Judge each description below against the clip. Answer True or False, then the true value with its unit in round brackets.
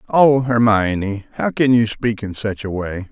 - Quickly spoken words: False (195 wpm)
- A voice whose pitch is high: False (110 Hz)